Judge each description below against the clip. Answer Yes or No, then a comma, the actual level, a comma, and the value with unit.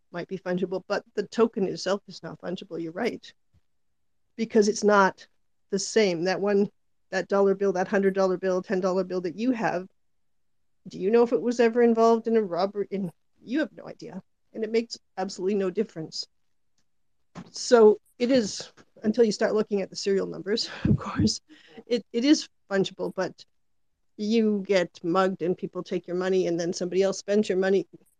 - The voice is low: No, high, 195 Hz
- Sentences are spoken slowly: No, average, 185 wpm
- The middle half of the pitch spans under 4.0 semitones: Yes, average, 2.9 semitones